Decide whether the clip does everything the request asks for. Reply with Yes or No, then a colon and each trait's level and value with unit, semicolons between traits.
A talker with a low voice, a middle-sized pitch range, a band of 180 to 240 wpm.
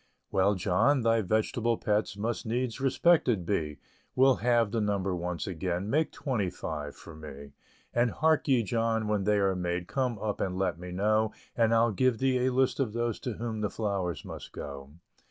Yes: low, 110 Hz; average, 4.5 semitones; average, 190 wpm